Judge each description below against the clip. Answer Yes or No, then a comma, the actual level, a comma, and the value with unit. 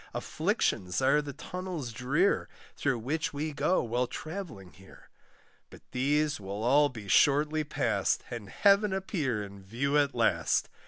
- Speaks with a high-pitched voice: No, medium, 140 Hz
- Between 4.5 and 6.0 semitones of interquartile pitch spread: Yes, average, 4.9 semitones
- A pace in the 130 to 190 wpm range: Yes, average, 145 wpm